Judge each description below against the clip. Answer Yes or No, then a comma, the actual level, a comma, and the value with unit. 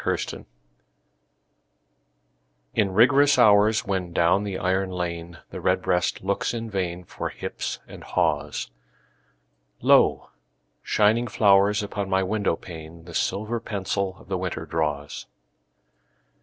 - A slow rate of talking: Yes, slow, 115 wpm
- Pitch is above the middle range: No, very low, 95 Hz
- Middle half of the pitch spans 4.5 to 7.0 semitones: No, average, 3.2 semitones